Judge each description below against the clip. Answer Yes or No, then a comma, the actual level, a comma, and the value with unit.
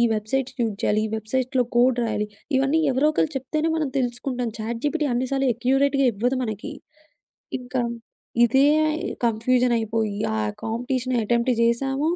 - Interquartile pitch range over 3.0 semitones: No, narrow, 2.6 semitones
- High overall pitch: Yes, very high, 250 Hz